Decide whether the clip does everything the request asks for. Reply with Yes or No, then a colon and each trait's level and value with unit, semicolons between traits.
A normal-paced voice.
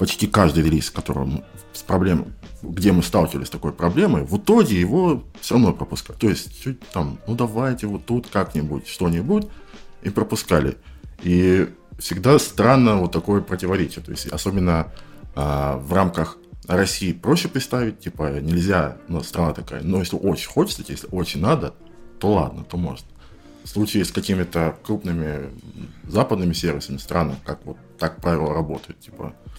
Yes: average, 150 wpm